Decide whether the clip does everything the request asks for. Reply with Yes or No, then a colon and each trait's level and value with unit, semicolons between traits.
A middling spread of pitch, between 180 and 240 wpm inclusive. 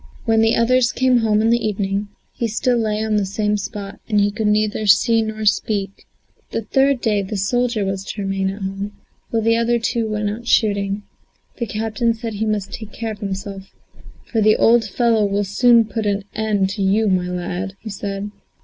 No: narrow, 2.2 semitones; average, 200 wpm